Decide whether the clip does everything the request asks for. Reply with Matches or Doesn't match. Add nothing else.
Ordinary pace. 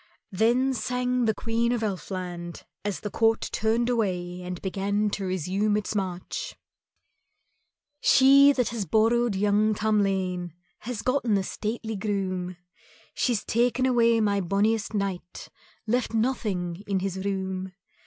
Doesn't match